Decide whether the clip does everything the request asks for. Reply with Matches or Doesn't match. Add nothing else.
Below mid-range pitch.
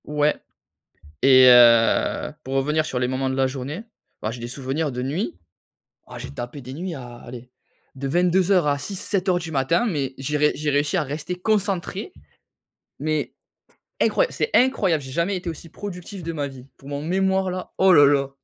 Doesn't match